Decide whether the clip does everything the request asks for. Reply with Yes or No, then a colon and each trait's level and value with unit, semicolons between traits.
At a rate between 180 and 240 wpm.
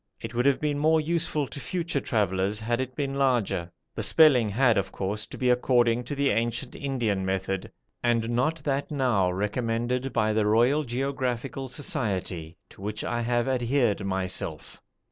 No: average, 165 wpm